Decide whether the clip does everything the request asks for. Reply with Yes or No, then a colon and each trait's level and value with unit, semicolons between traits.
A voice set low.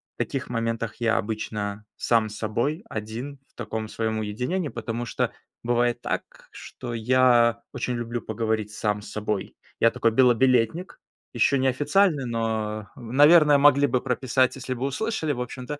Yes: low, 120 Hz